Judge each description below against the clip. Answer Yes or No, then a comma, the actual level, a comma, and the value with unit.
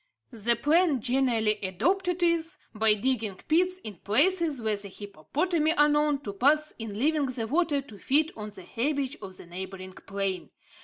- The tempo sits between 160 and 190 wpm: Yes, average, 165 wpm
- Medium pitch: No, very high, 255 Hz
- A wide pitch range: Yes, wide, 6.8 semitones